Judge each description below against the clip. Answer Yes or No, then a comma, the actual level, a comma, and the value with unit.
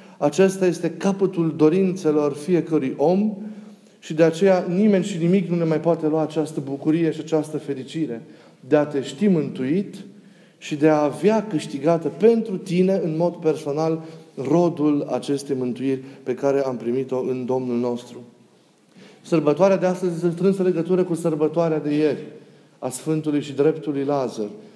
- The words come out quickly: No, average, 150 wpm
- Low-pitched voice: No, medium, 160 Hz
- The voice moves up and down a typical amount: Yes, average, 4.1 semitones